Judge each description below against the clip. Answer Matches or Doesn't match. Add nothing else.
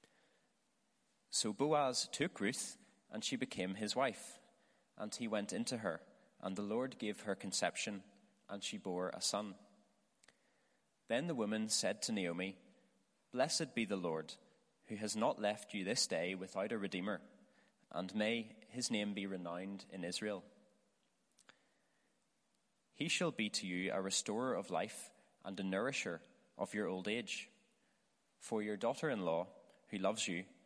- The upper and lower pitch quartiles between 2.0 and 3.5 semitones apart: Matches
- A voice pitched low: Matches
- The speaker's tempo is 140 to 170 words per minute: Matches